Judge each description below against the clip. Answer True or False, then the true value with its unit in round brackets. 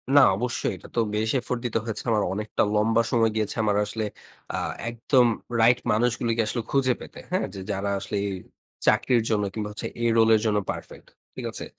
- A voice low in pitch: True (115 Hz)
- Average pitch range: False (2.0 semitones)